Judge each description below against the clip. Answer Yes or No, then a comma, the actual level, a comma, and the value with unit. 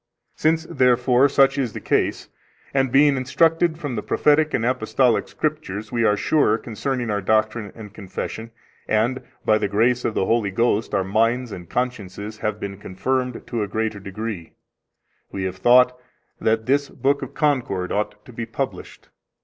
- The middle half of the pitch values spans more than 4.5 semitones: No, average, 3.9 semitones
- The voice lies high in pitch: No, low, 115 Hz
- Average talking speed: Yes, average, 165 wpm